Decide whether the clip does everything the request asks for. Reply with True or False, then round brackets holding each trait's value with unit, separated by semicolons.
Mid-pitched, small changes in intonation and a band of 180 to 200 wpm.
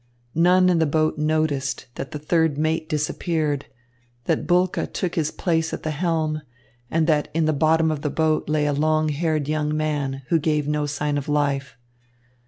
True (155 Hz; 1.5 semitones; 185 wpm)